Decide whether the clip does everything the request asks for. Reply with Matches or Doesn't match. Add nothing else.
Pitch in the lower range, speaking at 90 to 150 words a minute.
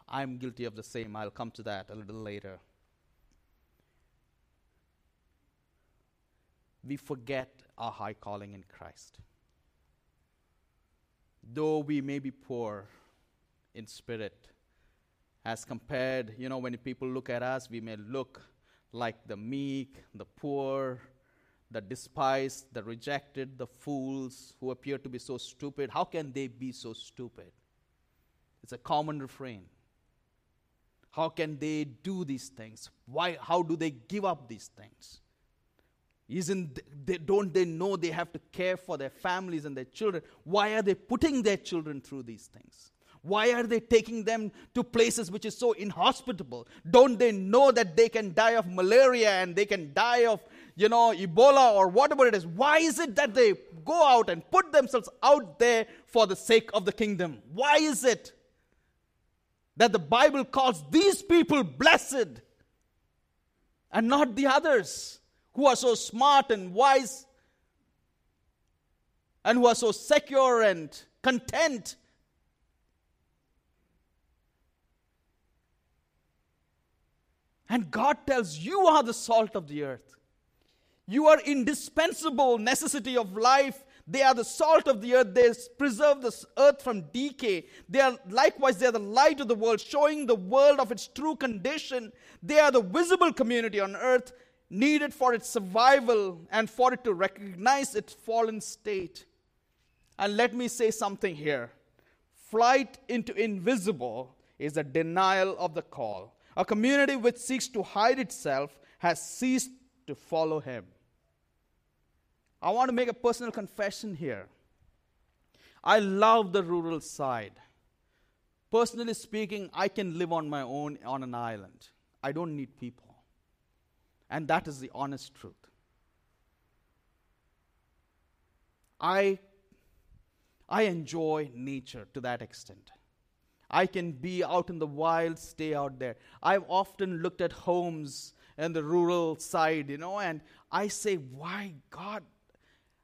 Doesn't match